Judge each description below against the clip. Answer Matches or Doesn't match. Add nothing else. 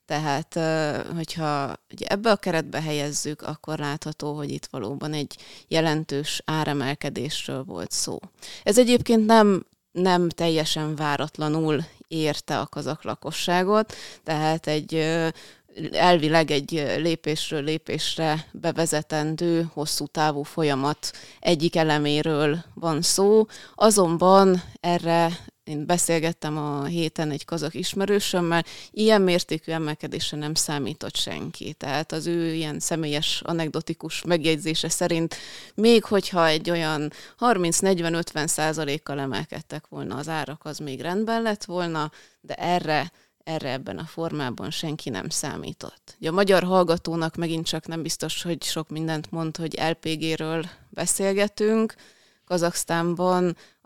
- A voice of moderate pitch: Matches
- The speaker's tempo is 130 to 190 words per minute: Doesn't match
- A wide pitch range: Doesn't match